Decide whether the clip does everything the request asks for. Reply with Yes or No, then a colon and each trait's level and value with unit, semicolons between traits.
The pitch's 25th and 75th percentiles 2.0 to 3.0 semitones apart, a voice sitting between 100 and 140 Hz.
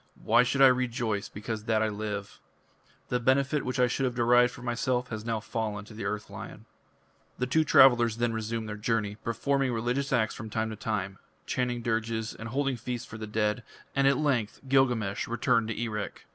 Yes: narrow, 2.4 semitones; low, 115 Hz